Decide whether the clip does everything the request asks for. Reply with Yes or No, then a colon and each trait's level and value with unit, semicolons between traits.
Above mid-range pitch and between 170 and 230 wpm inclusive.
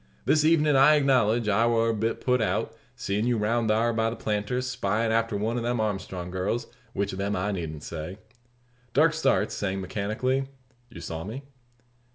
No: low, 110 Hz; average, 185 wpm